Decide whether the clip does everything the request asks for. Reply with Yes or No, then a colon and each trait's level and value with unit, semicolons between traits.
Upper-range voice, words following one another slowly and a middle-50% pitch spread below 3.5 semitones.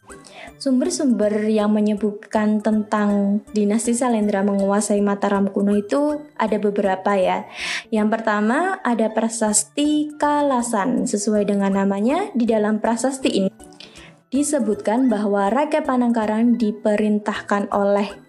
No: high, 215 Hz; average, 100 wpm; average, 3.1 semitones